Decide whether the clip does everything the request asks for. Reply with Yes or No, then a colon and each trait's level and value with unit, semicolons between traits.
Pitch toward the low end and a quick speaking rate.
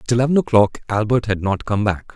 Yes: low, 110 Hz; fast, 225 wpm